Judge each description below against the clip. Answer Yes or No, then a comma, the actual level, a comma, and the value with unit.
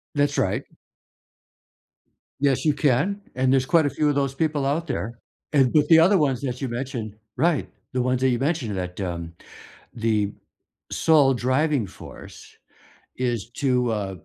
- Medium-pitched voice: No, low, 130 Hz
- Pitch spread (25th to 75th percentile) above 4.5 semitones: No, average, 3.8 semitones